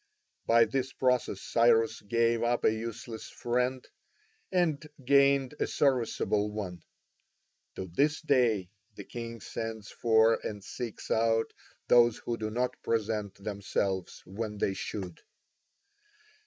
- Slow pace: Yes, slow, 120 wpm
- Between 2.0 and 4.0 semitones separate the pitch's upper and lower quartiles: Yes, average, 2.8 semitones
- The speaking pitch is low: Yes, low, 115 Hz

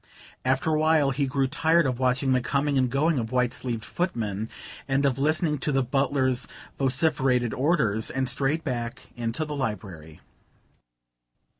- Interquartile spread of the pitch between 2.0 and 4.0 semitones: Yes, average, 2.9 semitones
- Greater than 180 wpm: No, average, 155 wpm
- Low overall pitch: Yes, low, 130 Hz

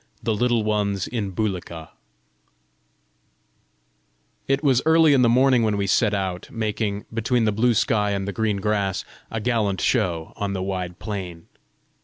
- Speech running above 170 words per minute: No, average, 155 wpm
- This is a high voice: No, low, 105 Hz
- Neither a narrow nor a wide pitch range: Yes, average, 3.1 semitones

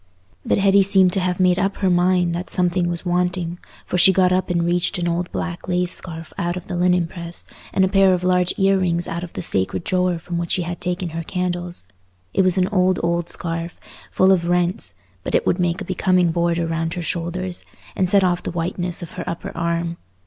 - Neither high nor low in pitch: Yes, medium, 175 Hz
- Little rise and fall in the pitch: Yes, narrow, 1.3 semitones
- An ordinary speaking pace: No, fast, 225 wpm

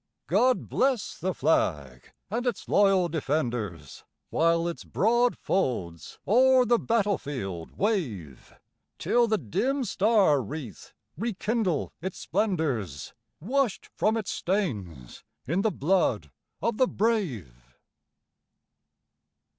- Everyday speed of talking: No, slow, 105 wpm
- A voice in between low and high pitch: Yes, medium, 180 Hz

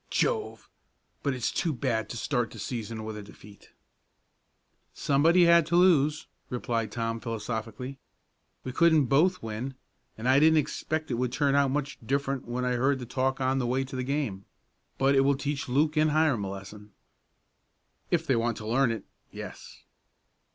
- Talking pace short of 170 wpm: No, average, 175 wpm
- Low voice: Yes, low, 130 Hz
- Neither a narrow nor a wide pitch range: Yes, average, 4.1 semitones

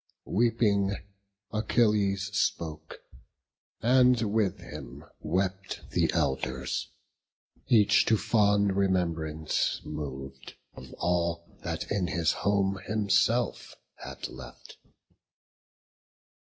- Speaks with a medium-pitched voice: No, very low, 95 Hz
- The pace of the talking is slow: Yes, slow, 85 wpm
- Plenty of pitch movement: No, average, 5.0 semitones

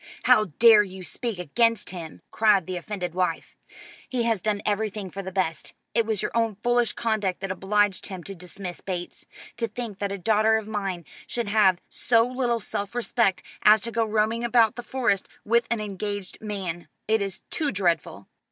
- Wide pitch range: No, average, 3.3 semitones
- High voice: Yes, high, 210 Hz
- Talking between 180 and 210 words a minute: Yes, average, 185 wpm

